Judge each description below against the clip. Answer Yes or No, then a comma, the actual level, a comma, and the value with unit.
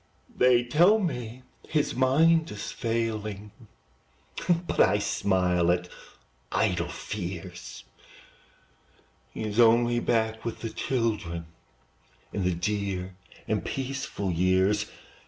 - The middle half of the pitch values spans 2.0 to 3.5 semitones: No, average, 4.8 semitones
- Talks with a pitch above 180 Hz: No, low, 110 Hz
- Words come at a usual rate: No, slow, 100 wpm